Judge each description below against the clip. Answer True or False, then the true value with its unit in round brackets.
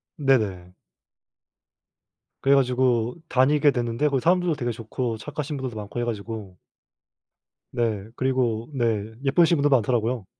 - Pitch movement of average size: True (3.5 semitones)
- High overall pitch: False (125 Hz)